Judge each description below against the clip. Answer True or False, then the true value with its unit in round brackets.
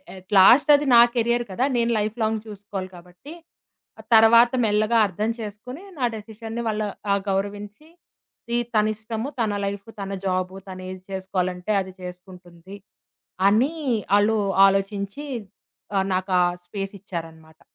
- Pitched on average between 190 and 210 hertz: True (205 Hz)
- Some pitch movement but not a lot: True (3.0 semitones)